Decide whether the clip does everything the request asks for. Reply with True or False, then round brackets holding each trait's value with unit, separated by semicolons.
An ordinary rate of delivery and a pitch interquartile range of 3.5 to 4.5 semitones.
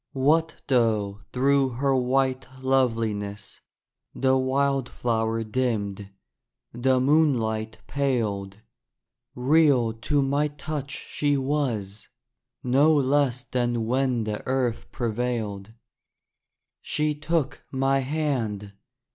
False (90 wpm; 3.8 semitones)